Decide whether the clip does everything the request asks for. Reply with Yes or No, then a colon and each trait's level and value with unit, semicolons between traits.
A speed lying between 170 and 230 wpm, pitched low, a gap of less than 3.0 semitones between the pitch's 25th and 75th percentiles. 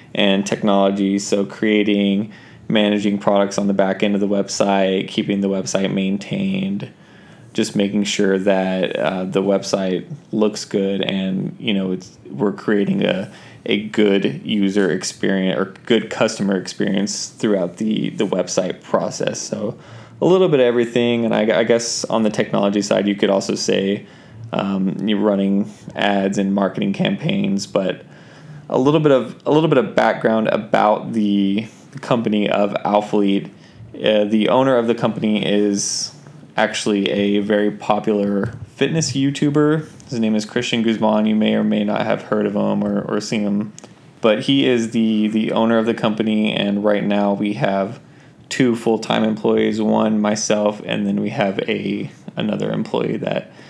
No: average, 160 wpm; low, 105 Hz; narrow, 2.5 semitones